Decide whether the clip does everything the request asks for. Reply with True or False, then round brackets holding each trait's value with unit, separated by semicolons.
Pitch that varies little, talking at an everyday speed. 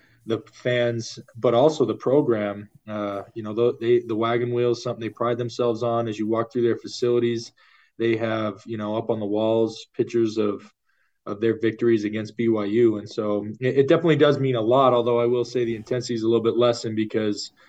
False (1.6 semitones; 210 wpm)